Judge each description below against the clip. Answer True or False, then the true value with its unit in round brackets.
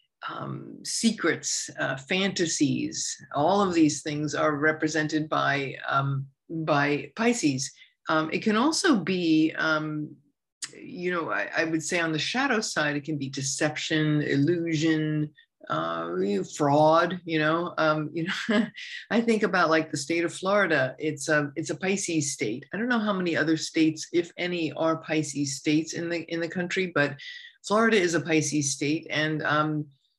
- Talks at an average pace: True (160 wpm)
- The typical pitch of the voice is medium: True (160 Hz)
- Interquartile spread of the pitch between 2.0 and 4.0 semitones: True (3.2 semitones)